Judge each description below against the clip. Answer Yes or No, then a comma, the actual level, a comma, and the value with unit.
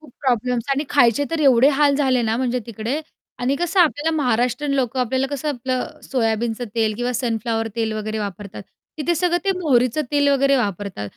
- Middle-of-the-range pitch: No, very high, 250 Hz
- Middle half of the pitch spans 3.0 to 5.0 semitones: Yes, average, 4.1 semitones